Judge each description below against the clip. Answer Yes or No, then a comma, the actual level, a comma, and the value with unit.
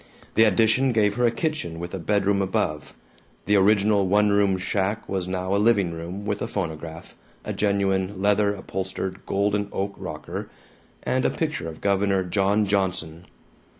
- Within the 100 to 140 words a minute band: No, average, 160 wpm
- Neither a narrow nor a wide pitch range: No, narrow, 1.8 semitones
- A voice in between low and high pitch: No, low, 100 Hz